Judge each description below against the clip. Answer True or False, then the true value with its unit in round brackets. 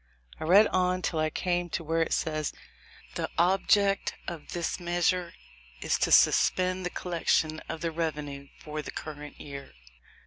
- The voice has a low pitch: False (165 Hz)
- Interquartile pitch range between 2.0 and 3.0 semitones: True (2.7 semitones)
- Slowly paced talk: False (160 wpm)